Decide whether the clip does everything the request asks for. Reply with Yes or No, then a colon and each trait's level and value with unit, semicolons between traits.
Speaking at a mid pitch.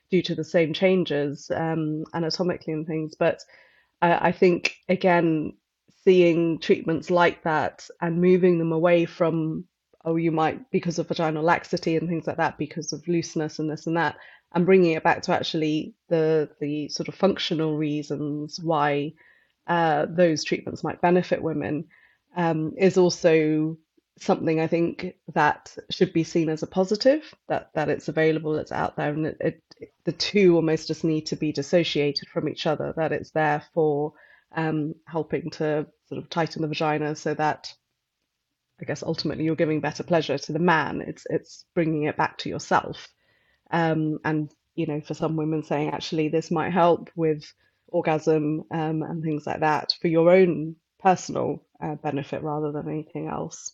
Yes: medium, 160 Hz